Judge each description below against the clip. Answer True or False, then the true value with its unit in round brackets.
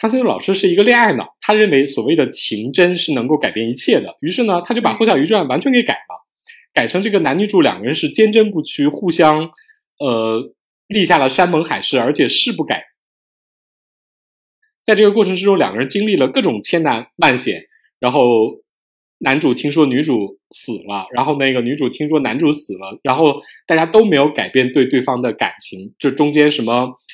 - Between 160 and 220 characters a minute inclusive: False (295 characters per minute)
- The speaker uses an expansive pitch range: True (7.6 semitones)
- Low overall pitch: False (165 Hz)